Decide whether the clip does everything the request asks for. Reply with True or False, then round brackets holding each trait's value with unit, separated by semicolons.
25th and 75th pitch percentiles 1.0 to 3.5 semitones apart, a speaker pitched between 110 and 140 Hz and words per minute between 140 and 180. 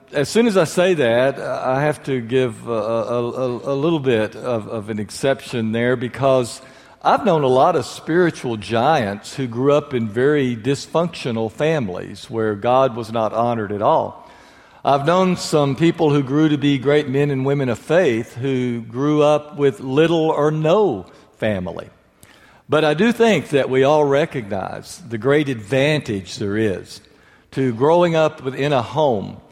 False (4.1 semitones; 135 Hz; 170 wpm)